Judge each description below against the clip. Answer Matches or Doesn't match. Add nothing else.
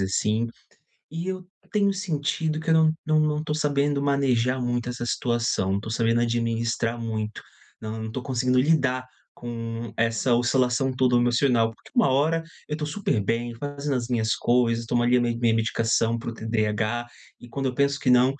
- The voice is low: Matches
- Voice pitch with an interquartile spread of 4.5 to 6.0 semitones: Doesn't match